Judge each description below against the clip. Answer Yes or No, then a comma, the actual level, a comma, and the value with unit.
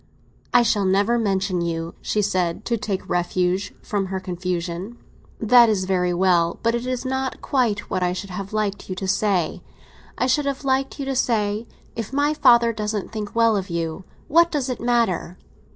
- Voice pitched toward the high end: Yes, high, 210 Hz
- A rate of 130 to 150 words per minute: No, average, 185 wpm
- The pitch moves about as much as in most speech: Yes, average, 4.4 semitones